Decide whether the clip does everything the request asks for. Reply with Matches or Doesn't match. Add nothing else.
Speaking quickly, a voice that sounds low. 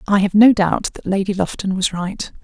Doesn't match